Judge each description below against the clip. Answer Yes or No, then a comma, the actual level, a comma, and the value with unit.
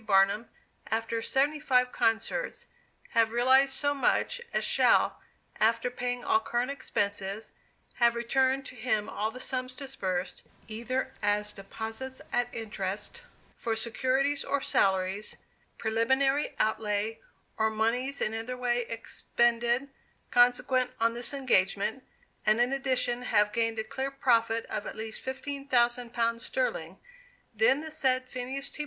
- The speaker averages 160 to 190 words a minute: No, slow, 135 wpm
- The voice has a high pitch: Yes, high, 240 Hz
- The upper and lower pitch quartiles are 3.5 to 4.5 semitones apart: No, average, 3.0 semitones